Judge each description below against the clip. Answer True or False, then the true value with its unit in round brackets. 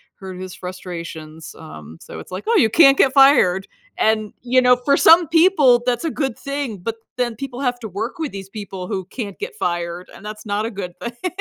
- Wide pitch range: True (6.4 semitones)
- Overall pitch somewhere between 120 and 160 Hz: False (220 Hz)